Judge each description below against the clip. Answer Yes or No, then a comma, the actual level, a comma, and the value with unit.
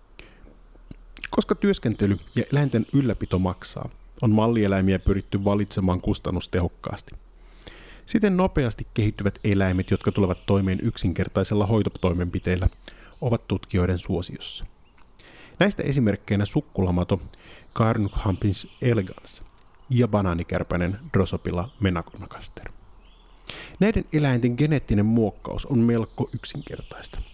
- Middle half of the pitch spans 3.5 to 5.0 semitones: Yes, average, 3.9 semitones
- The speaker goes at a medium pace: No, slow, 85 wpm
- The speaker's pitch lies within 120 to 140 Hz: No, low, 100 Hz